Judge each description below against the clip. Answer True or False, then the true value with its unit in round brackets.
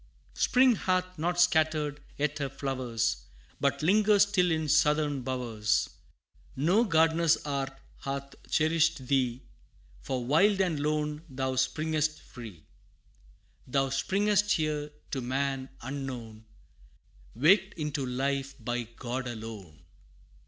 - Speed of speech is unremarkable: False (110 wpm)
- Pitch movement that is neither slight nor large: True (3.8 semitones)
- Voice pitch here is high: False (145 Hz)